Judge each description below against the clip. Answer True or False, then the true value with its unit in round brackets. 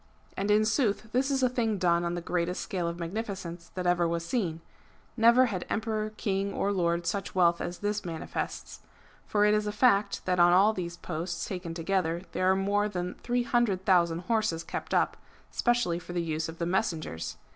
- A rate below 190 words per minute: False (200 wpm)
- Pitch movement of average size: True (3.6 semitones)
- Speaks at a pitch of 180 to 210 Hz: True (185 Hz)